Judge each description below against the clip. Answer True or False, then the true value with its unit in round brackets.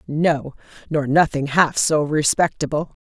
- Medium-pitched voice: True (150 Hz)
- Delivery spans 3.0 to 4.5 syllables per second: True (4.1 syllables/s)